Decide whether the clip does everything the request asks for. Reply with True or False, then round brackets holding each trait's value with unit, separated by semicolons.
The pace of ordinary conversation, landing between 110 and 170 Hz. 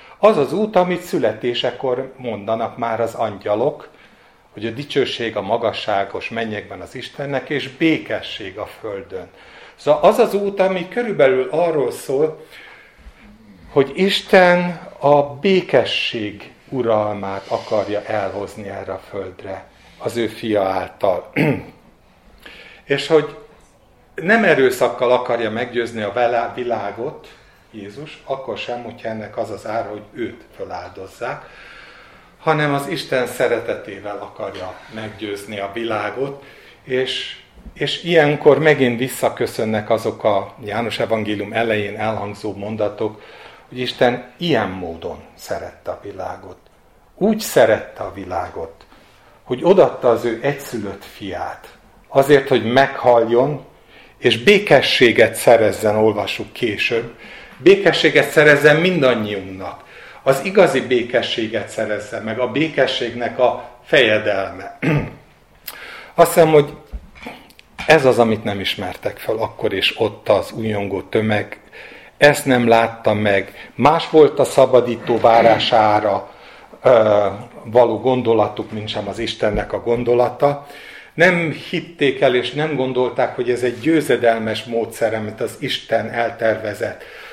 True (115 wpm; 125 Hz)